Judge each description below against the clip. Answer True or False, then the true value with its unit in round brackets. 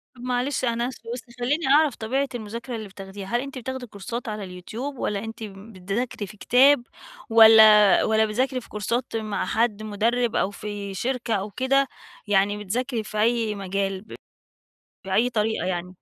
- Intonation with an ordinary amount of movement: True (3.3 semitones)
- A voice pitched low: False (220 Hz)